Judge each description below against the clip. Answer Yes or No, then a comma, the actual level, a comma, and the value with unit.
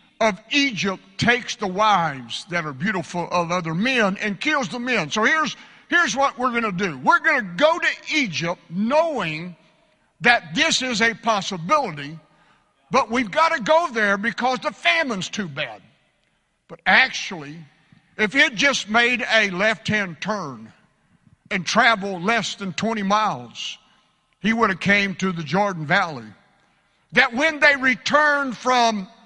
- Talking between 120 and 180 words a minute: Yes, average, 160 wpm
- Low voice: No, high, 215 Hz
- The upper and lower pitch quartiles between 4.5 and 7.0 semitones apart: Yes, wide, 5.6 semitones